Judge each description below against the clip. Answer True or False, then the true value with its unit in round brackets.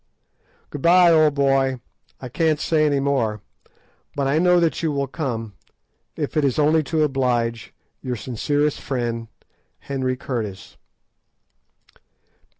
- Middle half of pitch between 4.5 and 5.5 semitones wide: False (3.5 semitones)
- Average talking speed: False (130 wpm)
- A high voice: False (140 Hz)